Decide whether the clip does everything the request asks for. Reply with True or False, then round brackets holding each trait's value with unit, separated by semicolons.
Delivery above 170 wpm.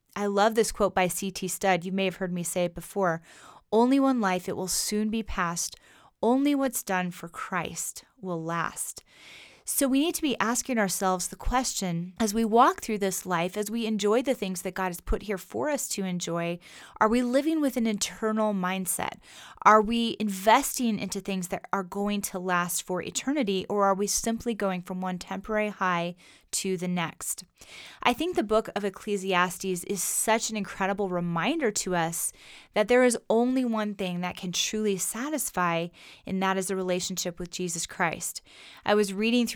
True (190 wpm)